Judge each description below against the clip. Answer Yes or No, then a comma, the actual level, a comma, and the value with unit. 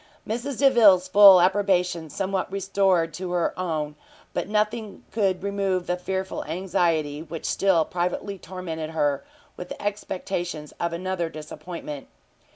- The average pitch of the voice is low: No, medium, 185 Hz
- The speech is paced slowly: Yes, slow, 130 wpm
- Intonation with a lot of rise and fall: No, average, 2.9 semitones